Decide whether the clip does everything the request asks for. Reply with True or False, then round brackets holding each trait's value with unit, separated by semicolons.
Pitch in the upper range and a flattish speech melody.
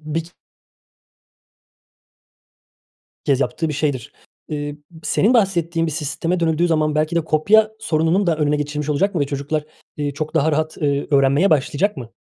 False (155 Hz; 2.3 semitones)